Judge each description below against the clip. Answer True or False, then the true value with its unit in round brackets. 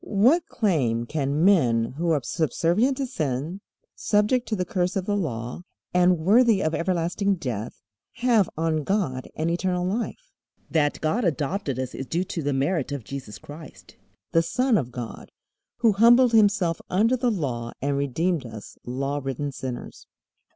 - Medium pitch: True (165 Hz)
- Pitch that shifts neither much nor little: False (6.8 semitones)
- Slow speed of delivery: False (160 wpm)